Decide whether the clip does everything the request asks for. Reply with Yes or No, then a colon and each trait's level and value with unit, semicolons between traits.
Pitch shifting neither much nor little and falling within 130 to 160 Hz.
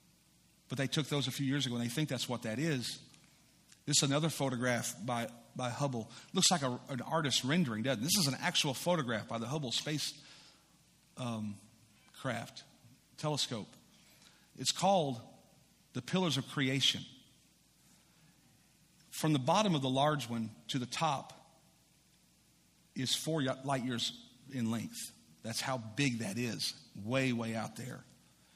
Yes: average, 4.5 semitones; low, 135 Hz